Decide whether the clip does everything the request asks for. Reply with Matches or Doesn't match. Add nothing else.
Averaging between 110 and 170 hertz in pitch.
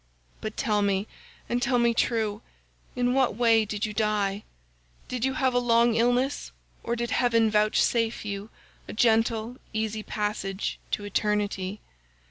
Doesn't match